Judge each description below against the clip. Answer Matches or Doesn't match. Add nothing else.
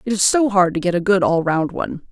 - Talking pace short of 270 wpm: Doesn't match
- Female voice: Matches